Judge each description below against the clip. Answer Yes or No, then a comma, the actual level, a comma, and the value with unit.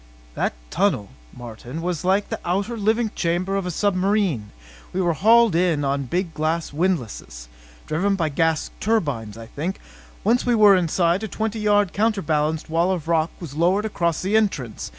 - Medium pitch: Yes, medium, 180 Hz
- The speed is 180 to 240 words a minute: No, average, 170 wpm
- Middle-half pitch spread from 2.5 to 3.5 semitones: No, average, 4.7 semitones